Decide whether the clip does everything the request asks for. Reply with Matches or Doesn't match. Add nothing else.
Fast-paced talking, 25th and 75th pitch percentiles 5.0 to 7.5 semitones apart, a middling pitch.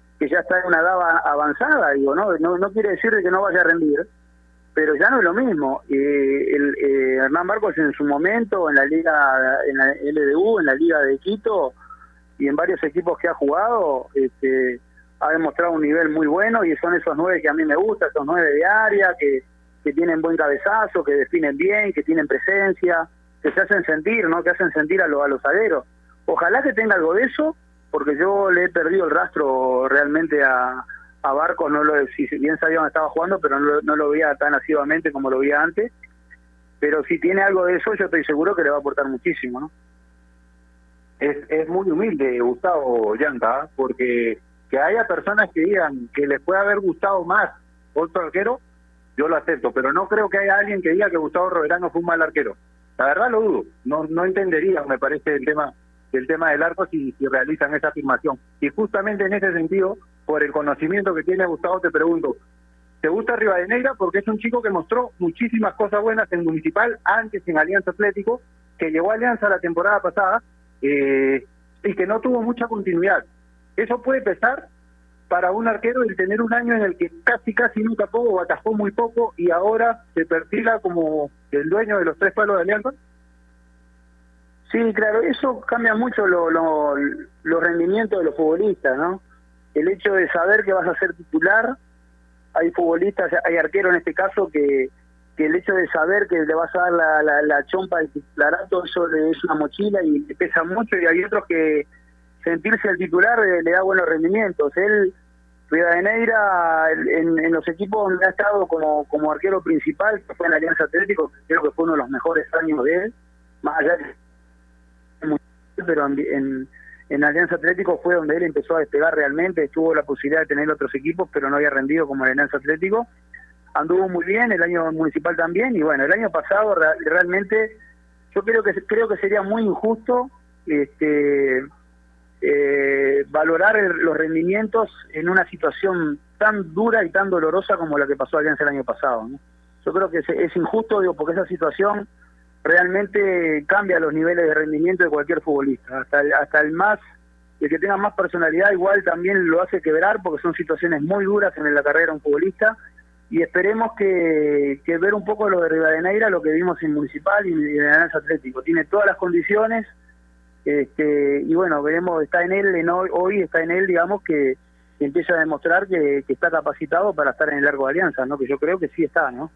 Matches